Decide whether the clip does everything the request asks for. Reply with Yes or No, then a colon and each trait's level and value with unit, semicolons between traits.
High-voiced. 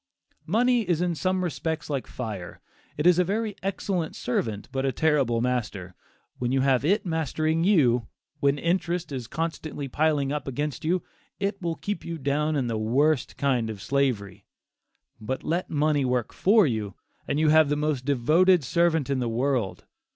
No: medium, 150 Hz